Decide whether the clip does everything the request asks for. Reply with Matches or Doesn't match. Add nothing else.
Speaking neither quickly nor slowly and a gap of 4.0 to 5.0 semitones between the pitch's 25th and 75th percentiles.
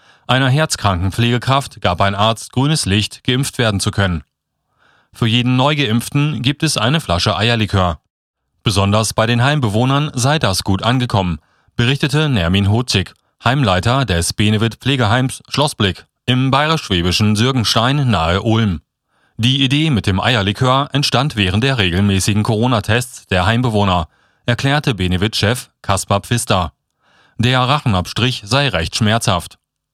Doesn't match